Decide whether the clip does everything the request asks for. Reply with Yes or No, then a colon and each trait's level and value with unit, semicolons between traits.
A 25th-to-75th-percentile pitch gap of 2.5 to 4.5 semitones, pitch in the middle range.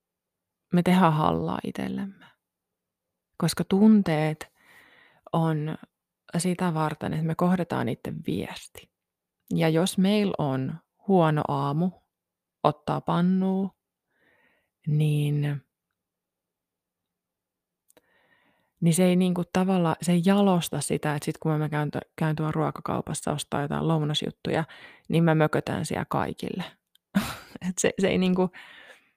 Yes: average, 3.1 semitones; medium, 165 Hz